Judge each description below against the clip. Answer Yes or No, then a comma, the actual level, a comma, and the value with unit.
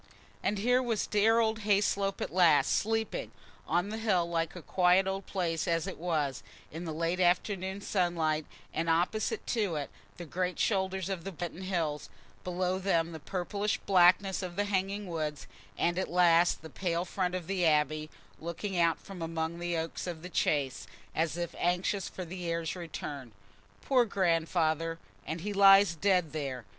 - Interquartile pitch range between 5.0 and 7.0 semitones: No, average, 2.9 semitones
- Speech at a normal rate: Yes, average, 170 wpm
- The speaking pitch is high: No, medium, 180 Hz